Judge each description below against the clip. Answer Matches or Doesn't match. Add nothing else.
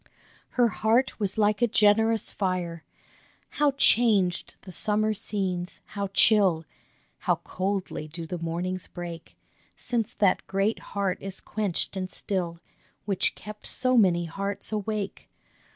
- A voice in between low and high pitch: Doesn't match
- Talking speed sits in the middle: Doesn't match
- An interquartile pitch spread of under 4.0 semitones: Matches